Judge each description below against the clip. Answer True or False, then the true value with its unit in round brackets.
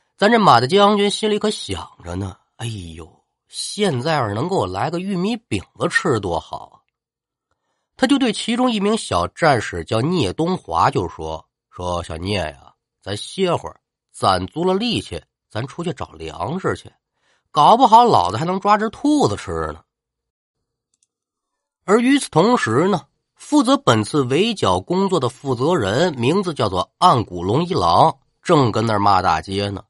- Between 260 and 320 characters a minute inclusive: False (230 characters per minute)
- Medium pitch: True (150 Hz)